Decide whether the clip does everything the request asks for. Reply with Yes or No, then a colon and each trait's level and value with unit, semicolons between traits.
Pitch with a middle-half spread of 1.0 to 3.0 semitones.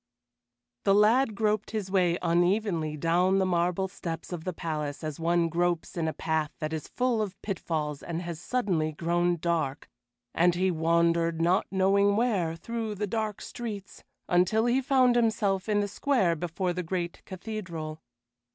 No: average, 3.8 semitones